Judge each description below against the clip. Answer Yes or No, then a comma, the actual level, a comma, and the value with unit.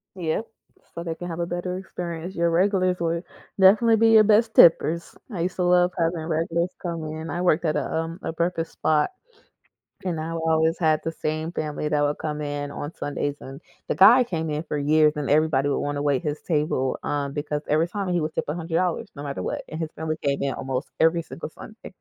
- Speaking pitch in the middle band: Yes, medium, 160 Hz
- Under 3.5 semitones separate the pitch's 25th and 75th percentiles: Yes, average, 2.7 semitones